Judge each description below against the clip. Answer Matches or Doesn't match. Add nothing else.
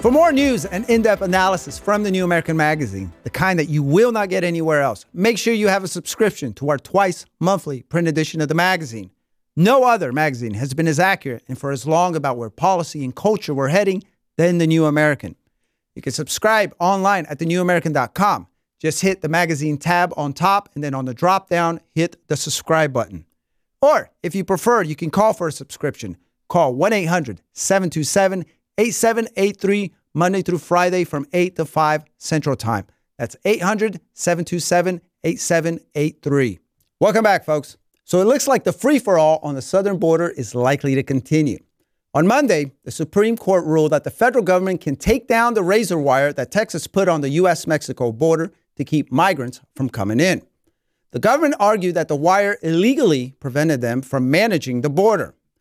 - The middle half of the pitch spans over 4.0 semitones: Matches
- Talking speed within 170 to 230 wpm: Matches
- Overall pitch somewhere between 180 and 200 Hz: Doesn't match